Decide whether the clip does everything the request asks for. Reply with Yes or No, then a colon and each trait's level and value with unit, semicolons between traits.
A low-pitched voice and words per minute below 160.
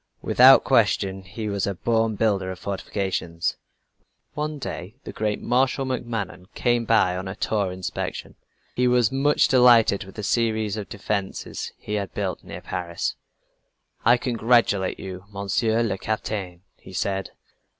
Yes: low, 105 Hz; average, 150 wpm